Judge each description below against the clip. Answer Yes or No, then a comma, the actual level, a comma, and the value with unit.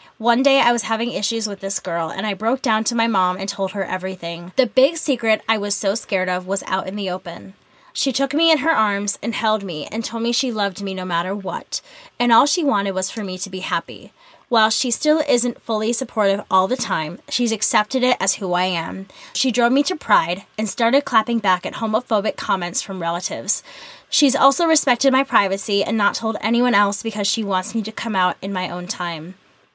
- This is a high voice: Yes, high, 215 Hz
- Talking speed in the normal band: No, fast, 225 wpm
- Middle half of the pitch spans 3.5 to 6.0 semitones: Yes, average, 4.4 semitones